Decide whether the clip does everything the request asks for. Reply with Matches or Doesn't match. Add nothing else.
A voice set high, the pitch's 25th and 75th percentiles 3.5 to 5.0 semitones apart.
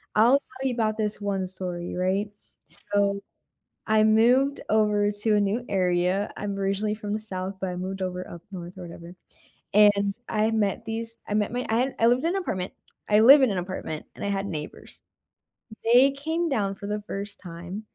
Doesn't match